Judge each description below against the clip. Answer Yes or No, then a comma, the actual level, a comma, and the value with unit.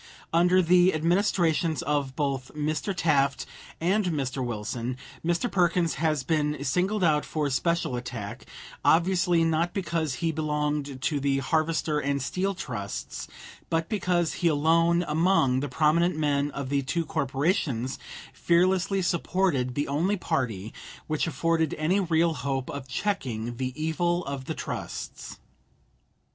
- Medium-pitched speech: Yes, medium, 155 Hz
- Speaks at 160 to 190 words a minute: No, slow, 135 wpm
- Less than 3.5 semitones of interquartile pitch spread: No, average, 3.9 semitones